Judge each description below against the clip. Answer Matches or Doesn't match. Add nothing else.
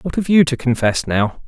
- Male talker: Matches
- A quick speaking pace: Matches